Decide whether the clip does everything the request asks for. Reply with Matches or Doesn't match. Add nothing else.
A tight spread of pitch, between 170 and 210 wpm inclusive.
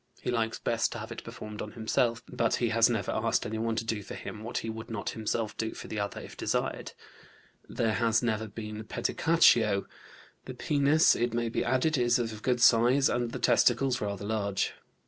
Matches